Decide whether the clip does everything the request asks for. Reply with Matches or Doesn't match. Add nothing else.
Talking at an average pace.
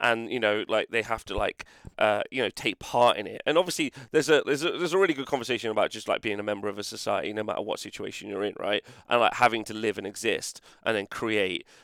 Doesn't match